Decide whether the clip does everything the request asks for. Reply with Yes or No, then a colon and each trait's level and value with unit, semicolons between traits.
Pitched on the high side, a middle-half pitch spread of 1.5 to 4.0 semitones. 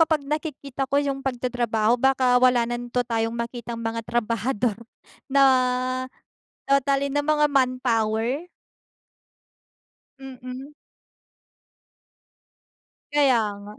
Yes: very high, 255 Hz; average, 2.9 semitones